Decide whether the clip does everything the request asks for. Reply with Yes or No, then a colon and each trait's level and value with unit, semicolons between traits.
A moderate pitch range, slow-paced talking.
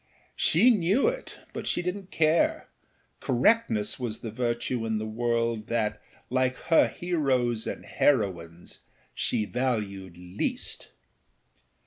No: wide, 6.4 semitones; slow, 115 wpm